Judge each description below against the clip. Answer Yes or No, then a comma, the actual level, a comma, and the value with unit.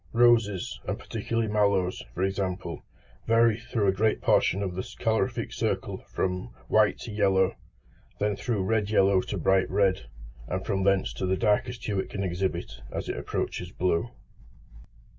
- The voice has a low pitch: Yes, low, 100 Hz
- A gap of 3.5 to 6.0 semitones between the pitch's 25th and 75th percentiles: No, narrow, 2.4 semitones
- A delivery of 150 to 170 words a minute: Yes, average, 160 wpm